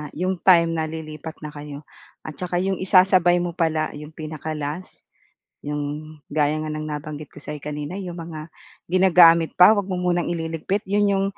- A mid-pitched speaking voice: Yes, medium, 160 Hz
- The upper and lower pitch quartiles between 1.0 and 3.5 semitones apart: Yes, average, 2.9 semitones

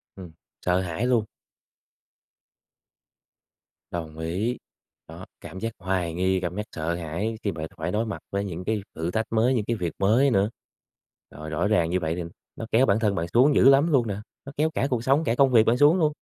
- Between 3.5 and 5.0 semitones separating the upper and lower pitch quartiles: No, wide, 5.6 semitones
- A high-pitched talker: No, low, 100 Hz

